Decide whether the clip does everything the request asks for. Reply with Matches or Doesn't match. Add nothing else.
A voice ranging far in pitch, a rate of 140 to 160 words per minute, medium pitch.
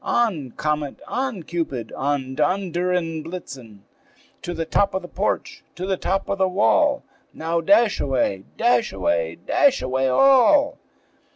Matches